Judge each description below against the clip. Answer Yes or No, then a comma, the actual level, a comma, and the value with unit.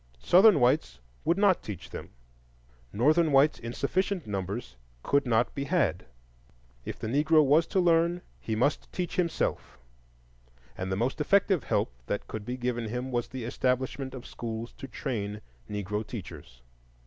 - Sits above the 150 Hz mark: No, low, 125 Hz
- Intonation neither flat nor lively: No, wide, 6.2 semitones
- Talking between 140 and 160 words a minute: Yes, average, 155 wpm